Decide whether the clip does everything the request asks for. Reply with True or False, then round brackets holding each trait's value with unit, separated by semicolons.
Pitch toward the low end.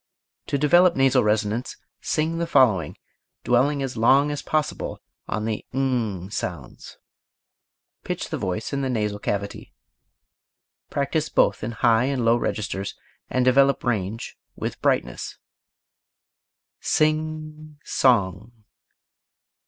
True (125 Hz)